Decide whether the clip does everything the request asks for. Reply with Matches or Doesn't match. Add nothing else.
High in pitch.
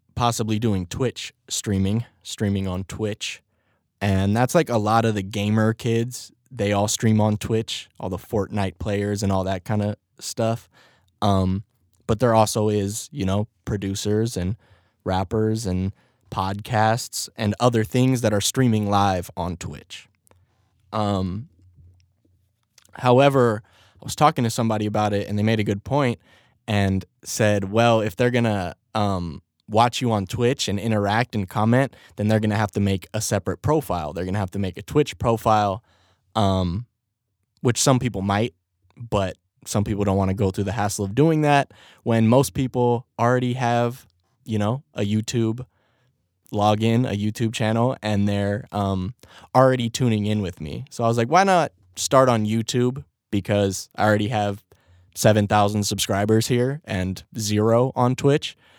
Doesn't match